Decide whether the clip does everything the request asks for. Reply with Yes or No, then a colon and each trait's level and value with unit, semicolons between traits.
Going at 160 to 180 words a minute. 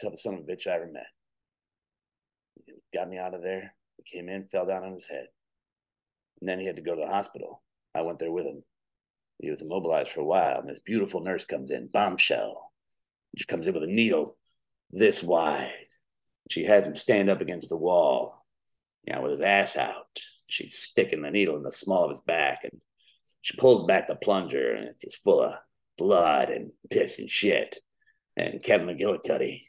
No: average, 200 wpm